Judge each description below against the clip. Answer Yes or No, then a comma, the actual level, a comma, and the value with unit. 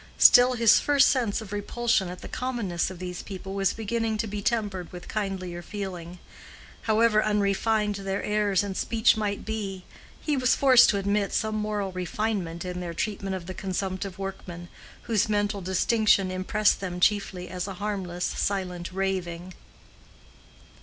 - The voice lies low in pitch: No, high, 200 Hz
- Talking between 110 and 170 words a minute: Yes, average, 155 wpm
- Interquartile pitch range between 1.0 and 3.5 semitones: Yes, narrow, 2.6 semitones